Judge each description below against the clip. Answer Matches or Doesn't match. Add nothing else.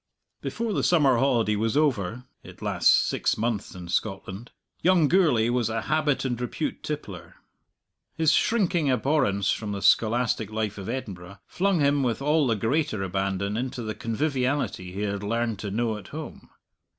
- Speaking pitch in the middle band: Doesn't match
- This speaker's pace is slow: Doesn't match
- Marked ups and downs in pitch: Matches